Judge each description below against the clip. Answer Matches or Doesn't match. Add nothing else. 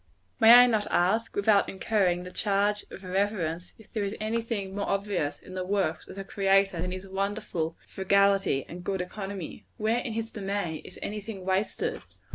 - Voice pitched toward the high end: Matches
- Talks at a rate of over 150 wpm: Matches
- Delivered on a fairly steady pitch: Matches